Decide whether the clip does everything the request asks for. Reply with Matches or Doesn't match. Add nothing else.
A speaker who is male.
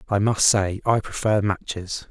Matches